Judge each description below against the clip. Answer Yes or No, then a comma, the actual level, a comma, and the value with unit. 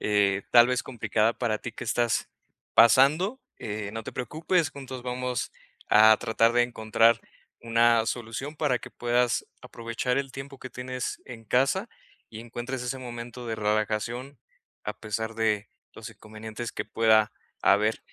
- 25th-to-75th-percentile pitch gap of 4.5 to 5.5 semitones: No, narrow, 2.5 semitones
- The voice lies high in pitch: No, low, 120 Hz